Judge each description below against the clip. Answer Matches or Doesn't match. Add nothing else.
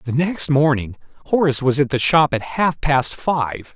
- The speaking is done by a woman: Doesn't match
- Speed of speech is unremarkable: Matches